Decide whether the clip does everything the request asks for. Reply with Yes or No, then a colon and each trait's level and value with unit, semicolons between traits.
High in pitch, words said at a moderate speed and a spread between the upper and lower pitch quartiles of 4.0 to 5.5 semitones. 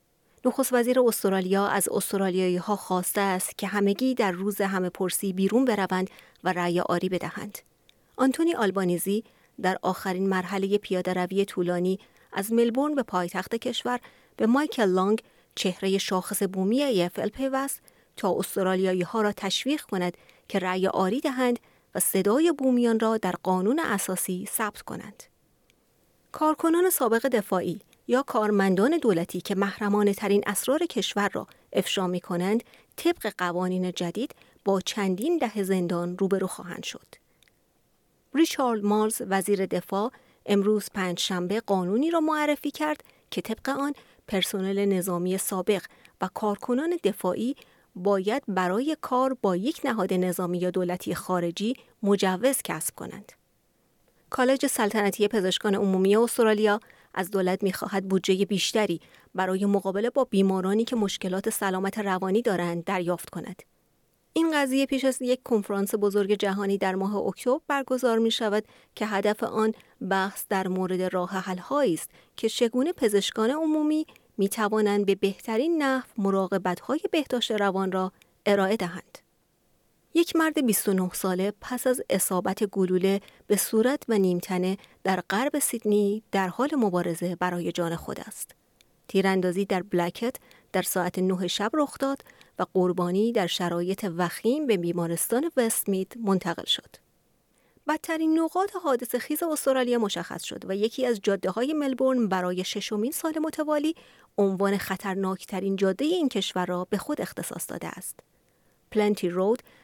Yes: high, 200 Hz; average, 135 wpm; average, 4.5 semitones